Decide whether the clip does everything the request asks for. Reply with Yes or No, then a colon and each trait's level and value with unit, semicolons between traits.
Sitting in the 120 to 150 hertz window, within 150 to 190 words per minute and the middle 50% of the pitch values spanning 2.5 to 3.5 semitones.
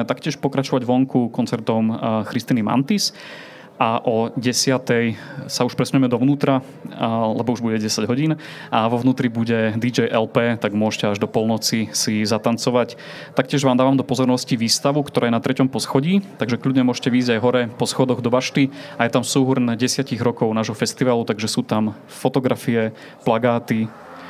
Yes: low, 125 Hz; average, 160 wpm; average, 2.8 semitones